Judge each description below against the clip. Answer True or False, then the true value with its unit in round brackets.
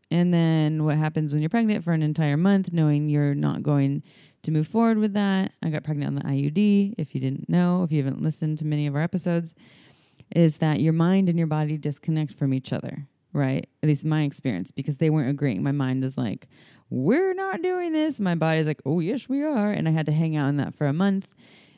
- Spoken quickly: True (235 wpm)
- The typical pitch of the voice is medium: True (155 Hz)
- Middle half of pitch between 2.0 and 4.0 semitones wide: True (3.5 semitones)